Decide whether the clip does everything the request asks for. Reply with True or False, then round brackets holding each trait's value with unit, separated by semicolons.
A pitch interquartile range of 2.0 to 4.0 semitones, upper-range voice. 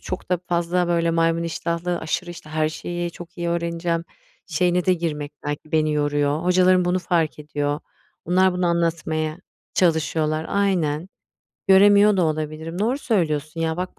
False (2.4 semitones; 170 Hz)